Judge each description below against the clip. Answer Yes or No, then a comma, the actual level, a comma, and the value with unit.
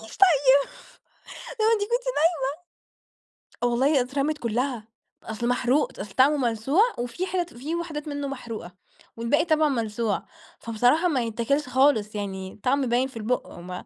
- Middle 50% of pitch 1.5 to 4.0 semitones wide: No, average, 4.6 semitones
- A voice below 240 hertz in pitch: No, very high, 255 Hz